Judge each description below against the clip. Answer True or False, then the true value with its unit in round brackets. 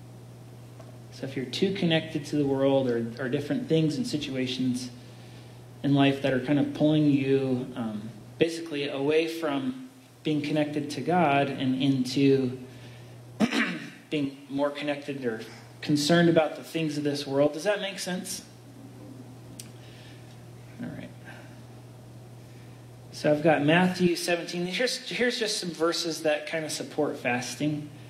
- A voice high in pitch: False (135 Hz)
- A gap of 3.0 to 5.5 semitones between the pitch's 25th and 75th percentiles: True (3.7 semitones)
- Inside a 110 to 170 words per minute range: True (135 wpm)